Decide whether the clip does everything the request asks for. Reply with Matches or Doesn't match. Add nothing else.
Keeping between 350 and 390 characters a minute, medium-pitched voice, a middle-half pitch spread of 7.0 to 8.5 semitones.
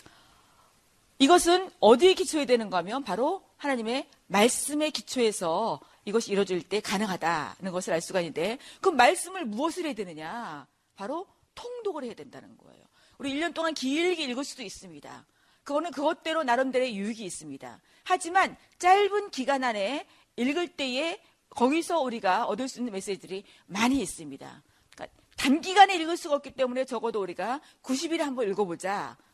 Doesn't match